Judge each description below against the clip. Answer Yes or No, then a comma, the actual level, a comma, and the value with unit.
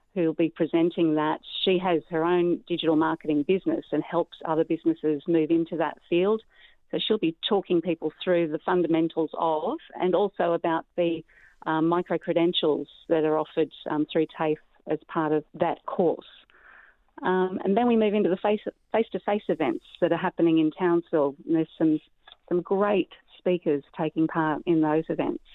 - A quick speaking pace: No, average, 170 wpm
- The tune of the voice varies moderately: No, narrow, 2.2 semitones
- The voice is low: No, medium, 170 Hz